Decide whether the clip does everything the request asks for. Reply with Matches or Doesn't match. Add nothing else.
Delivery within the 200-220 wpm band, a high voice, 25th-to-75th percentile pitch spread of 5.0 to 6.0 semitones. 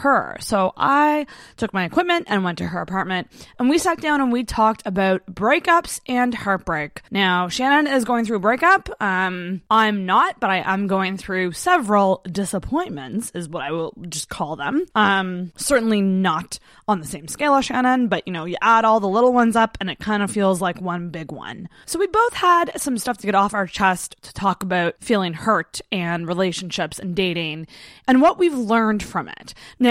Matches